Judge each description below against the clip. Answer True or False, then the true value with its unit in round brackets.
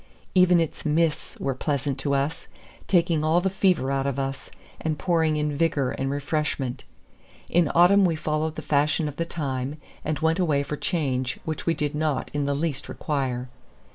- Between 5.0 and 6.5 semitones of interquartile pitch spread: False (2.9 semitones)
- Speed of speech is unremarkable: True (180 wpm)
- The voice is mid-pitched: True (150 Hz)